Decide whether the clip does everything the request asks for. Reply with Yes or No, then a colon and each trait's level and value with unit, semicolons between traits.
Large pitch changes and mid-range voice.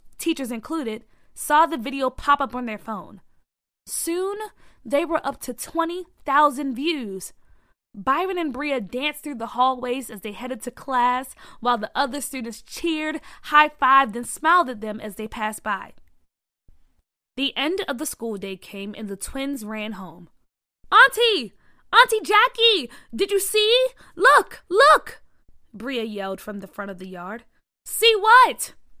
No: wide, 6.8 semitones; very high, 260 Hz